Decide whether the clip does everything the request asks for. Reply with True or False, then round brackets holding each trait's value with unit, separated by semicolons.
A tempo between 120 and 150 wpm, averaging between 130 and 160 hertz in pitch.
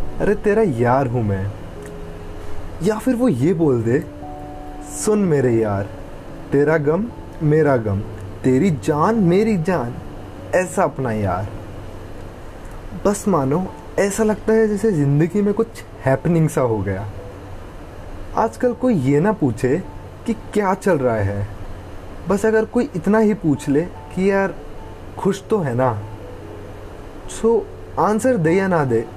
True (140 wpm; 135 Hz)